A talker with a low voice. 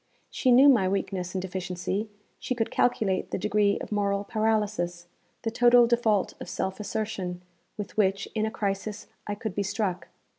No: high, 205 Hz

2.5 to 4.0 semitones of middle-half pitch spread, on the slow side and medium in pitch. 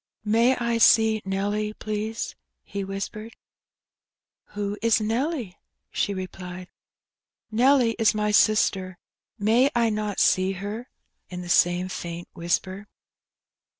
No: average, 3.1 semitones; slow, 115 wpm; high, 210 Hz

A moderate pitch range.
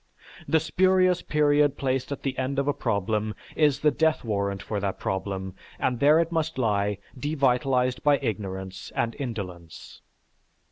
No: wide, 6.5 semitones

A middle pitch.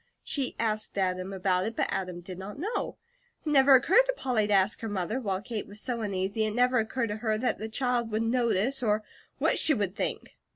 No: high, 220 Hz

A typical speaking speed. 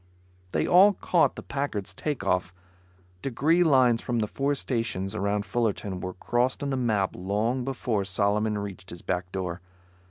Yes: average, 155 wpm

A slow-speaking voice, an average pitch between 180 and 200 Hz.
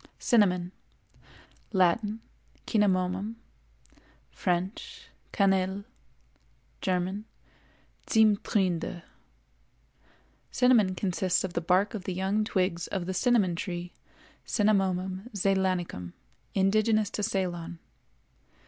Yes: slow, 70 wpm; high, 190 Hz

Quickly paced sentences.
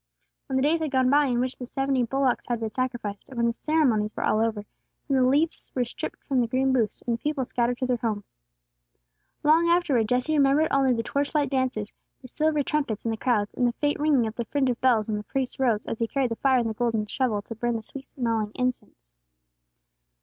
Yes: fast, 235 wpm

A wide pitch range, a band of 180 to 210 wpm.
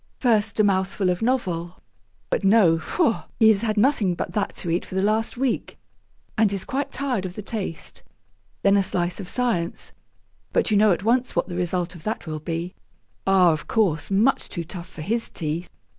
No: average, 4.2 semitones; average, 200 wpm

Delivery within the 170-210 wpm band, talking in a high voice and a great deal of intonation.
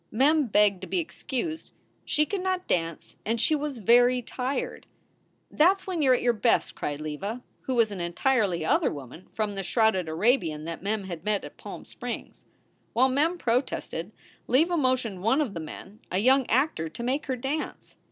Yes: average, 190 wpm; high, 235 Hz; wide, 6.3 semitones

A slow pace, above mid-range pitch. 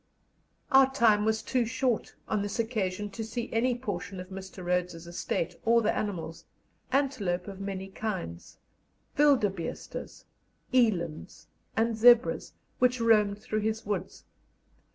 Yes: slow, 130 wpm; high, 210 Hz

